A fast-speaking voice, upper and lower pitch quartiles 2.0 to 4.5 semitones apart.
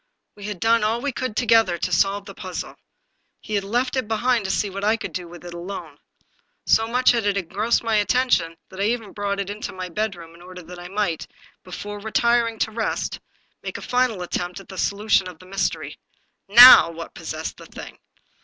Yes: fast, 210 wpm; average, 3.7 semitones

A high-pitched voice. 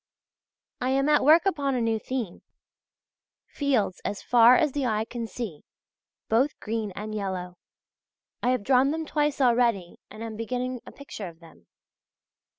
Yes: high, 240 Hz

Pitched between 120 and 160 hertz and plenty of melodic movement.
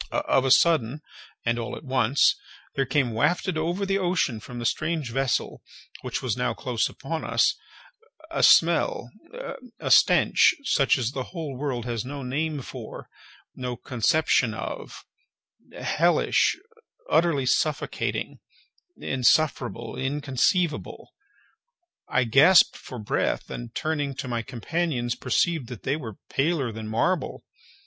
No: low, 135 Hz; average, 4.8 semitones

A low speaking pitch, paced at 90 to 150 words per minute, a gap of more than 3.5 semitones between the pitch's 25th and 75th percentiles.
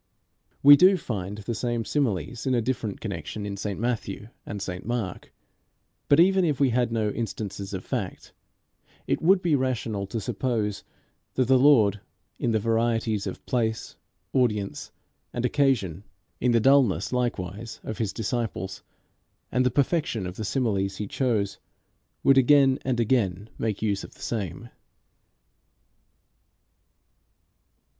Yes: low, 115 Hz; average, 140 wpm; average, 4.1 semitones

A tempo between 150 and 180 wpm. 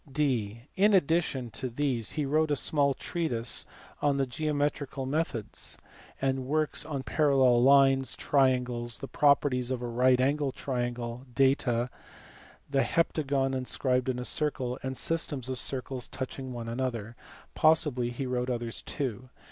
No: slow, 135 wpm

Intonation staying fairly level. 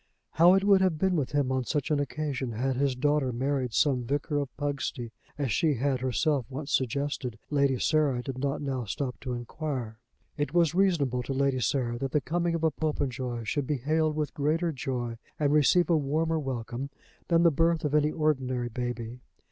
No: average, 3.3 semitones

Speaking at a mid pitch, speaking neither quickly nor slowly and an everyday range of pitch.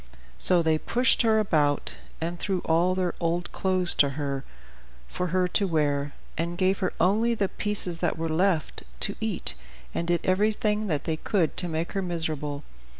Yes: medium, 175 Hz; average, 175 wpm; average, 3.4 semitones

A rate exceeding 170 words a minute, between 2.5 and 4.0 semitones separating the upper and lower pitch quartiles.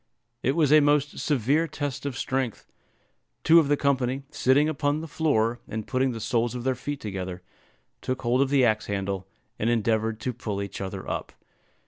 No: average, 185 wpm; average, 4.6 semitones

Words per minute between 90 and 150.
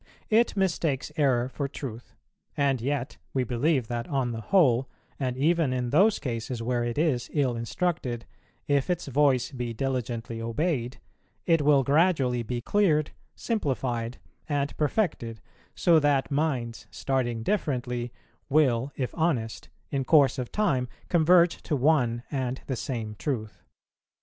Yes: average, 140 wpm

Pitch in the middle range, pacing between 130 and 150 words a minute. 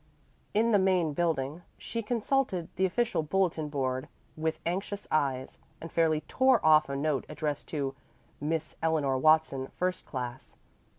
Yes: medium, 160 Hz; average, 140 wpm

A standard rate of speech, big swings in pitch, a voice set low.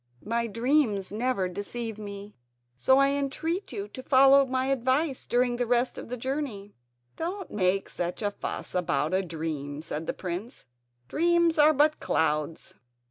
No: average, 155 wpm; wide, 6.3 semitones; high, 235 Hz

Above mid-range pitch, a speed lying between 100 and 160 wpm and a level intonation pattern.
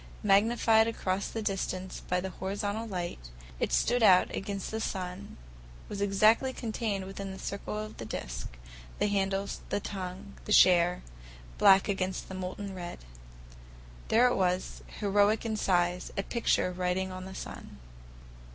Yes: high, 195 Hz; average, 145 wpm; narrow, 2.3 semitones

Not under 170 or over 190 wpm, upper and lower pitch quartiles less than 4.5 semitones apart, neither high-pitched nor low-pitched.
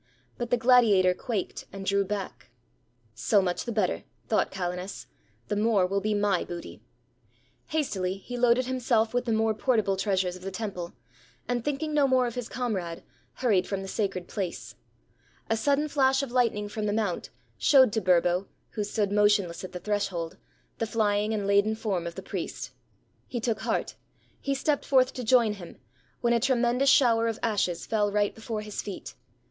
No: average, 180 wpm; average, 3.8 semitones; high, 210 Hz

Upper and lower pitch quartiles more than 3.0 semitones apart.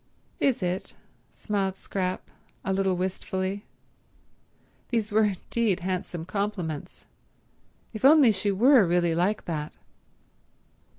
No: average, 2.7 semitones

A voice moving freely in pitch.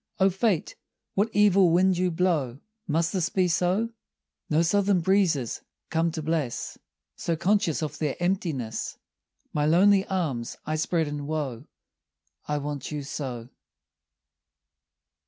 No: average, 4.2 semitones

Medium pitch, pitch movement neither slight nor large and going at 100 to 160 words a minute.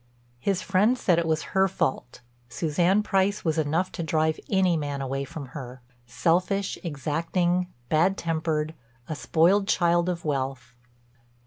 Yes: medium, 165 Hz; average, 4.0 semitones; slow, 135 wpm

